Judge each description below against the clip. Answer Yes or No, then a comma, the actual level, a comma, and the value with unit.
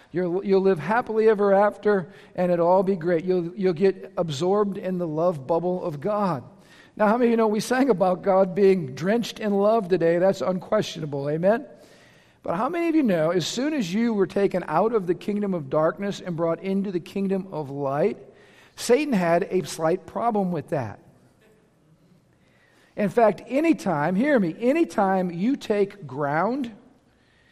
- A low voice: No, high, 195 Hz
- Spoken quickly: No, average, 170 wpm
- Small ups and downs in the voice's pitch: No, average, 3.5 semitones